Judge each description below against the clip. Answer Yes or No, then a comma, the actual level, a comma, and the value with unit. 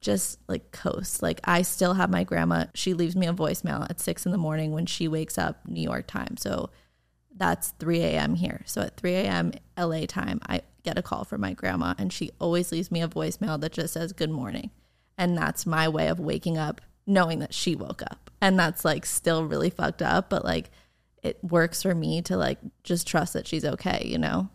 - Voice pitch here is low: No, medium, 160 Hz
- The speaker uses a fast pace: Yes, fast, 220 wpm